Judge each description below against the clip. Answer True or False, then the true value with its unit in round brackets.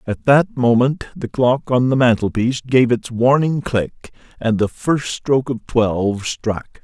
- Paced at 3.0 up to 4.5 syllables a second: True (4.1 syllables/s)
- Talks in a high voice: False (120 Hz)